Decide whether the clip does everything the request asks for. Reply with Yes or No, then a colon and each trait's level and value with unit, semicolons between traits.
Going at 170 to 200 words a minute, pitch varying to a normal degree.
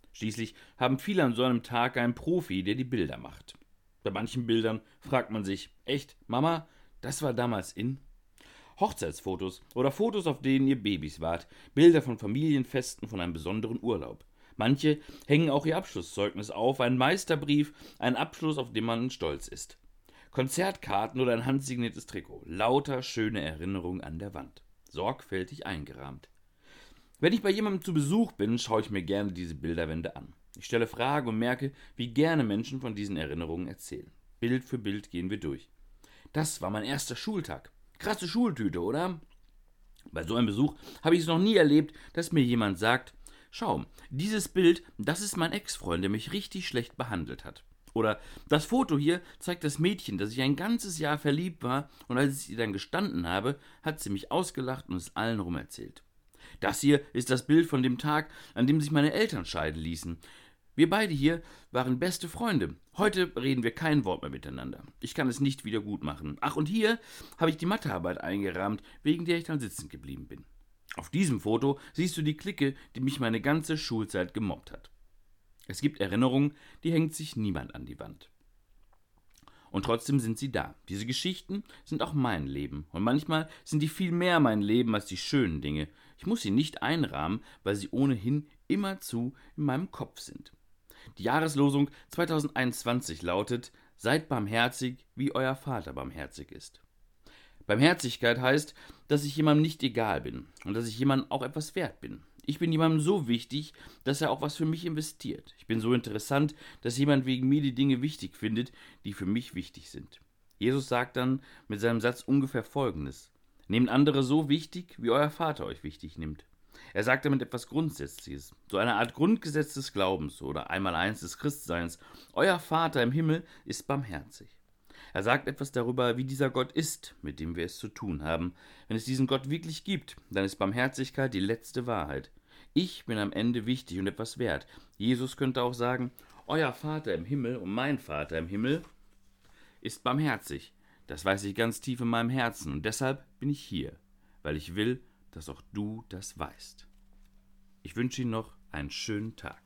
No: average, 180 wpm; wide, 7.0 semitones